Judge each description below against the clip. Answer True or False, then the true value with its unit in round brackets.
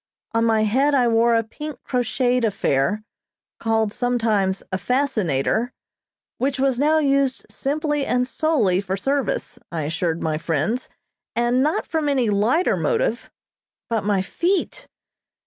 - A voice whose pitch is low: False (240 Hz)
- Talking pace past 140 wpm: False (135 wpm)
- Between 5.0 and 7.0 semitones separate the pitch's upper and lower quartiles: True (5.3 semitones)